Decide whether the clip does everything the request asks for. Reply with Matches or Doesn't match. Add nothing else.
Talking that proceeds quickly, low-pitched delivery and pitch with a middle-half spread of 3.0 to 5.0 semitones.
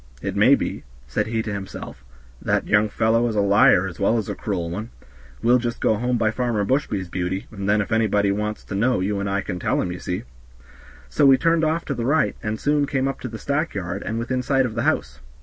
Matches